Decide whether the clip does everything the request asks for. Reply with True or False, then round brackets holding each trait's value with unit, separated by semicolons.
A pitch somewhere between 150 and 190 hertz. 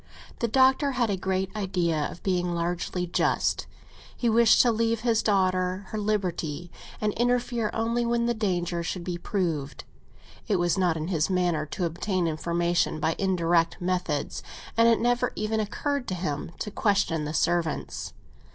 True (185 Hz)